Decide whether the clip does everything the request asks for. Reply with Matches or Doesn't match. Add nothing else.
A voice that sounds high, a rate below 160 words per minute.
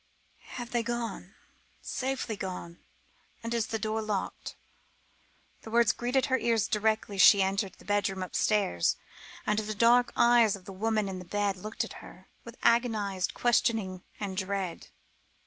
Matches